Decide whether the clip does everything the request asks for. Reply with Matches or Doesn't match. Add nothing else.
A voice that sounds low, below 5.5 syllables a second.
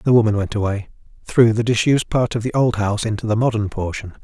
Doesn't match